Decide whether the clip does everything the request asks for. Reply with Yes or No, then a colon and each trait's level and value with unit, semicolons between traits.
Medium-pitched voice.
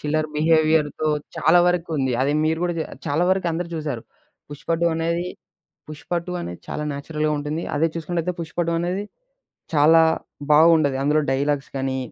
Yes: medium, 155 Hz